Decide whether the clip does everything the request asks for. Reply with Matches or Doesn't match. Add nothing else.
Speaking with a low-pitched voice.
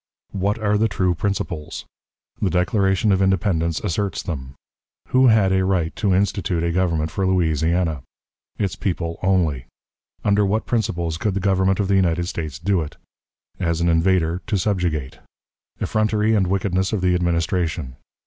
Matches